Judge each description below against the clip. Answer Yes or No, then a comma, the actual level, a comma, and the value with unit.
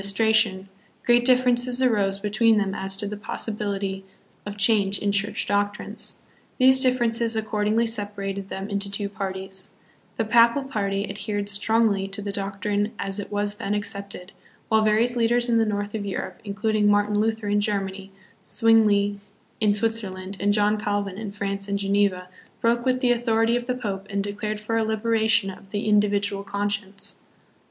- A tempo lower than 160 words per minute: No, average, 165 wpm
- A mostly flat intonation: Yes, narrow, 2.0 semitones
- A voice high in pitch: Yes, high, 205 Hz